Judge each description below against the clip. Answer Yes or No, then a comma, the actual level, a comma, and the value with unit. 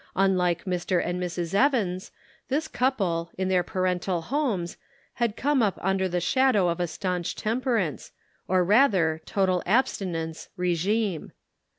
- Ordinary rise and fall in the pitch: Yes, average, 3.9 semitones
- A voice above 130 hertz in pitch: Yes, medium, 185 Hz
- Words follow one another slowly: Yes, slow, 130 wpm